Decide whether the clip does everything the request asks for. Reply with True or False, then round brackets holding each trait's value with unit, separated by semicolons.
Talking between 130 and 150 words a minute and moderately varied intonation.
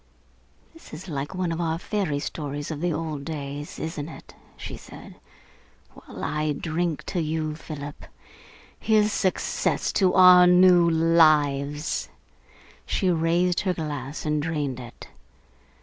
True (135 wpm; 3.2 semitones)